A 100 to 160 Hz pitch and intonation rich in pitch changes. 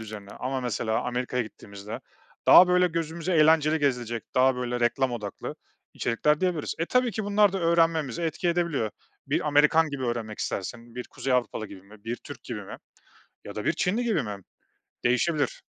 Yes: low, 135 Hz; wide, 5.9 semitones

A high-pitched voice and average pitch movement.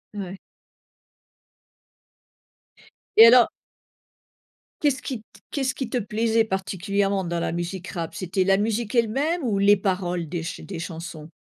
Yes: high, 200 Hz; average, 4.2 semitones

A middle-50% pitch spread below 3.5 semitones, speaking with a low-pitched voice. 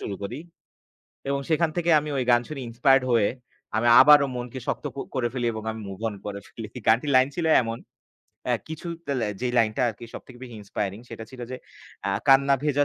No: average, 3.8 semitones; low, 125 Hz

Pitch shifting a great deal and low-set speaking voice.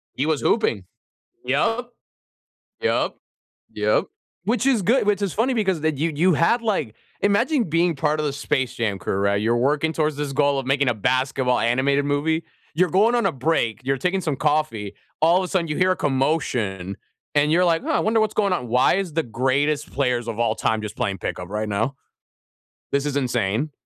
No: wide, 6.2 semitones; medium, 145 Hz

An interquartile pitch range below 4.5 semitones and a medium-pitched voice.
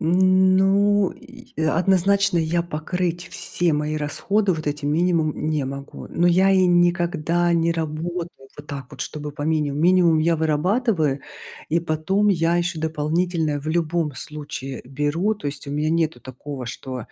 Yes: average, 3.1 semitones; medium, 165 Hz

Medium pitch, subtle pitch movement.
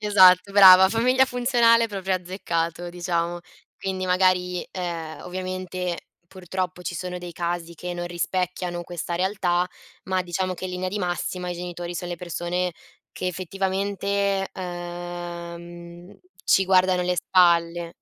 Yes: medium, 180 Hz; narrow, 1.4 semitones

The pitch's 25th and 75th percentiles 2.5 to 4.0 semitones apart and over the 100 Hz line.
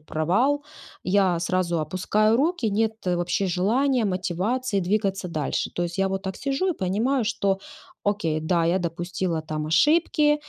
No: average, 4.5 semitones; high, 190 Hz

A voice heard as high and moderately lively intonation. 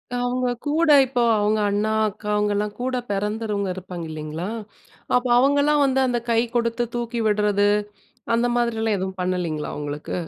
Yes: high, 215 Hz; average, 4.0 semitones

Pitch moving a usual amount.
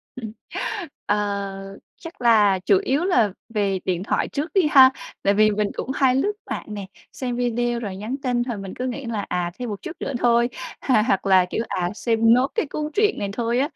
Yes: average, 4.4 semitones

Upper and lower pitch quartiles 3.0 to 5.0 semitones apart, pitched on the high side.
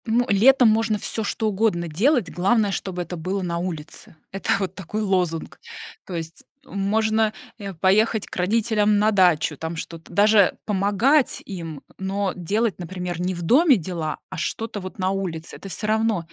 Yes: average, 3.6 semitones; high, 195 Hz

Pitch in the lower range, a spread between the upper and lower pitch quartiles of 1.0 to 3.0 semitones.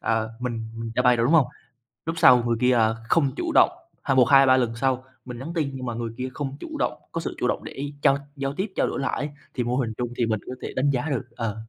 Yes: low, 125 Hz; average, 2.7 semitones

